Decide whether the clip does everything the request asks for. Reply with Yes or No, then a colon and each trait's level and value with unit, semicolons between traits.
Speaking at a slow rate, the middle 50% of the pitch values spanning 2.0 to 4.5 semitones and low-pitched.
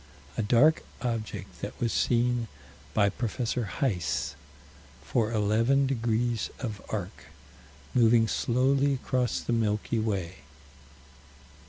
Yes: slow, 105 wpm; narrow, 2.5 semitones; low, 115 Hz